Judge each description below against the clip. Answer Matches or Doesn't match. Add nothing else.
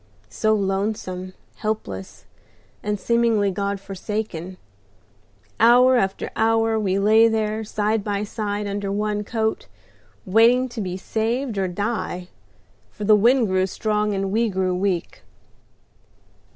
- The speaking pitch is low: Doesn't match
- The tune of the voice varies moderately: Doesn't match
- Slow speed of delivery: Matches